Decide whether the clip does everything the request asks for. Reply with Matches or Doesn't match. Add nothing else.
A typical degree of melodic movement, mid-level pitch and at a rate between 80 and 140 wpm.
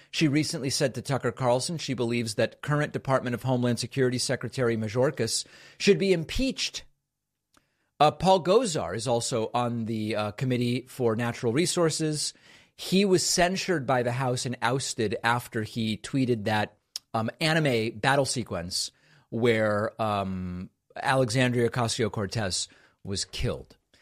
Doesn't match